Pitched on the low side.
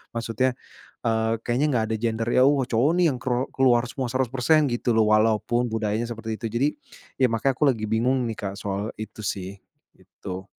Yes: low, 115 Hz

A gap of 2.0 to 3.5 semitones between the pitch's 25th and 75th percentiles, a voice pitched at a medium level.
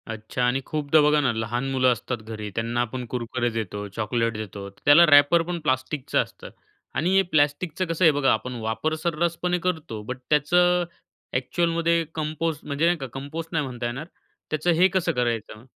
No: wide, 5.5 semitones; medium, 145 Hz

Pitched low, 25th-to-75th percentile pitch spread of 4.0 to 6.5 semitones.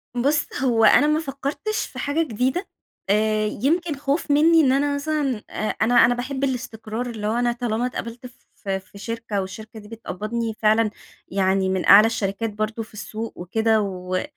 No: high, 230 Hz; average, 4.3 semitones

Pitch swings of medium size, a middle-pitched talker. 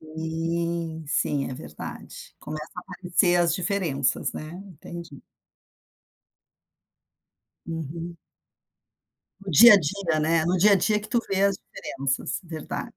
Yes: average, 3.1 semitones; medium, 170 Hz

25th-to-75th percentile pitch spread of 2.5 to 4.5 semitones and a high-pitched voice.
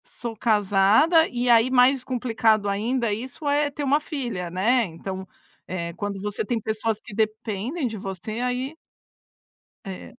Yes: average, 4.1 semitones; high, 225 Hz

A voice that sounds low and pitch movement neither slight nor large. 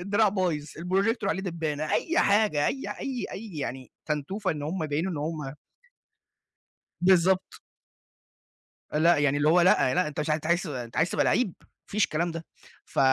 No: medium, 170 Hz; average, 4.1 semitones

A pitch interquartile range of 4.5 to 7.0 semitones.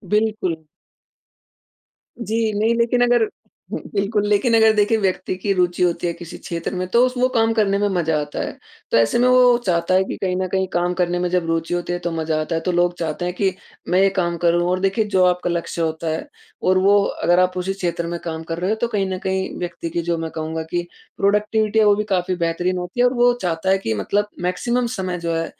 No: average, 3.3 semitones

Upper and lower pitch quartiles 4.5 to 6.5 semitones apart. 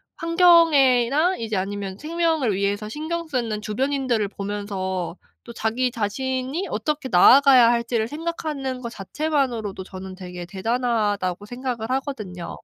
Yes: wide, 5.6 semitones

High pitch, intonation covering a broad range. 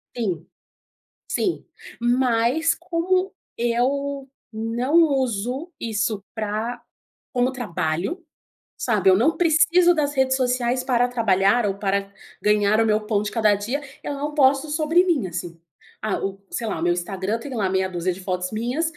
Yes: high, 235 Hz; wide, 5.7 semitones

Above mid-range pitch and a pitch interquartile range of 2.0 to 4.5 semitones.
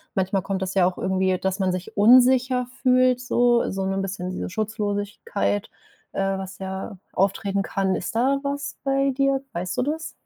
No: high, 200 Hz; average, 4.9 semitones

